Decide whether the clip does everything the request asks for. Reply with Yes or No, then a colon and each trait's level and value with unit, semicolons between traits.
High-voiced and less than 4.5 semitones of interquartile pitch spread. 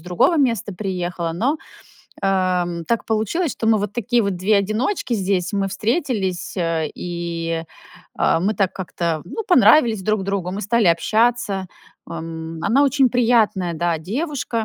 No: high, 200 Hz; average, 4.9 semitones